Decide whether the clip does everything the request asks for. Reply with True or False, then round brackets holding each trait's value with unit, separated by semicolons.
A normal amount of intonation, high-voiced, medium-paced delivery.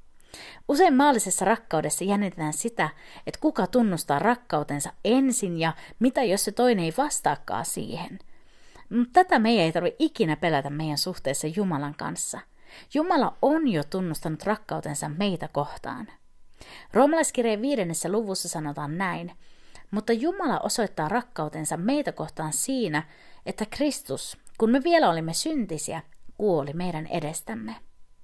False (7.1 semitones; 200 Hz; 125 wpm)